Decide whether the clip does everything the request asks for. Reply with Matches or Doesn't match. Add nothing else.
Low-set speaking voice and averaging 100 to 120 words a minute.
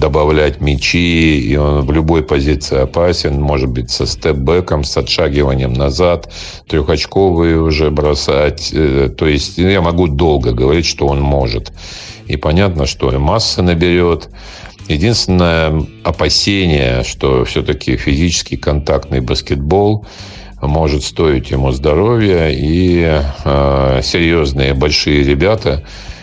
Matches